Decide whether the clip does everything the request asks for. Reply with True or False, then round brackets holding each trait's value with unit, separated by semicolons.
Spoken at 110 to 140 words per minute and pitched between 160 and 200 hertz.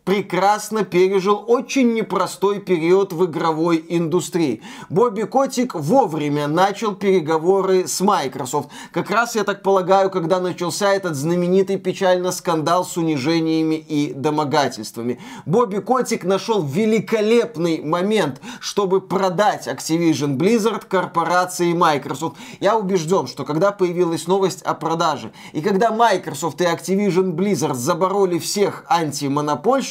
True (115 wpm; 185 Hz)